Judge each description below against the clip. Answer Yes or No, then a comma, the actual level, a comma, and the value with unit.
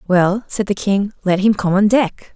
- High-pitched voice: Yes, high, 200 Hz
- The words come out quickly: Yes, fast, 230 wpm